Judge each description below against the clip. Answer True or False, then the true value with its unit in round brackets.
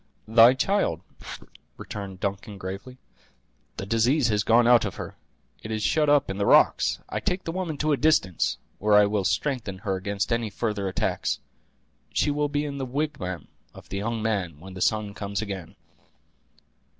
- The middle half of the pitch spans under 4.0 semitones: False (5.5 semitones)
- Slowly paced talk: False (175 wpm)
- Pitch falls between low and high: False (110 Hz)